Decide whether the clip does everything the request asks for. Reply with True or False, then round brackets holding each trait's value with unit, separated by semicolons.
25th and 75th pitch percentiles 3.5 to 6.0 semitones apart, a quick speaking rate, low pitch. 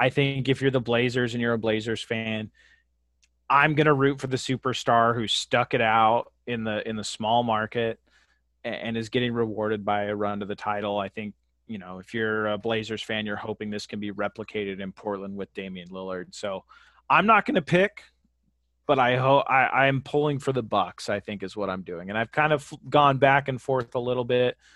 True (4.0 semitones; 215 wpm; 110 Hz)